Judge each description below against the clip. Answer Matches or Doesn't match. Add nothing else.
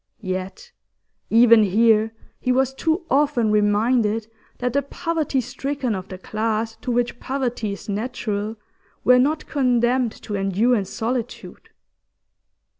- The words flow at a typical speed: Doesn't match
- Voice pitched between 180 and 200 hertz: Doesn't match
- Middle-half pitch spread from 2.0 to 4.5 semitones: Matches